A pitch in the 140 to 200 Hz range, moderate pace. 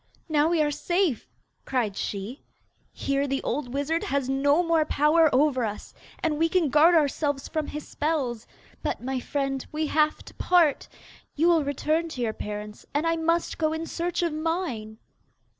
No: very high, 300 Hz; average, 175 wpm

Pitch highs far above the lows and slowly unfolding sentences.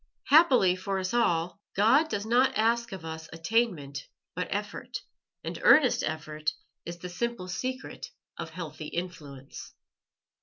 Yes: wide, 6.4 semitones; slow, 130 wpm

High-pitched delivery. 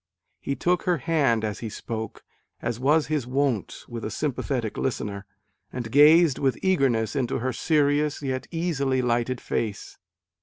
No: low, 130 Hz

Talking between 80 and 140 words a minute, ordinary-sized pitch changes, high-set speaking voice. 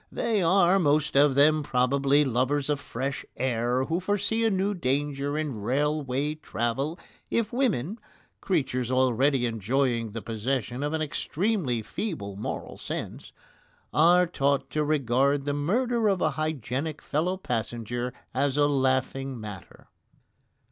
No: slow, 135 wpm; average, 3.9 semitones; medium, 140 Hz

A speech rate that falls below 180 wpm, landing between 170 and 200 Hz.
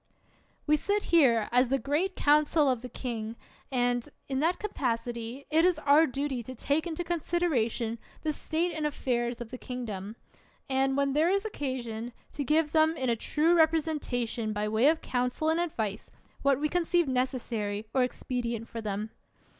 No: average, 170 wpm; very high, 265 Hz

